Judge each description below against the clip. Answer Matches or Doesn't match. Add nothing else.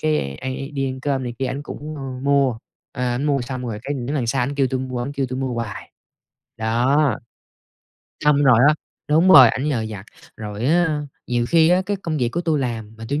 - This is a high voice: Doesn't match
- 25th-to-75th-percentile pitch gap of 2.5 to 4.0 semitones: Matches